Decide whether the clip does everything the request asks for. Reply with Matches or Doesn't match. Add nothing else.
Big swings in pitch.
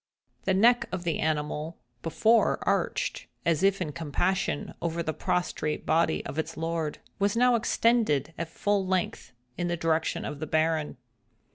Doesn't match